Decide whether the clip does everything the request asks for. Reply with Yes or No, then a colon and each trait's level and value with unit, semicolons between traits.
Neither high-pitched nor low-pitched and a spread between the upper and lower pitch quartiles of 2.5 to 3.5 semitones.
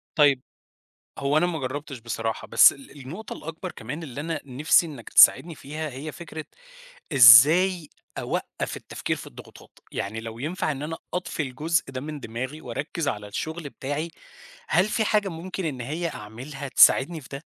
No: medium, 150 Hz; average, 4.0 semitones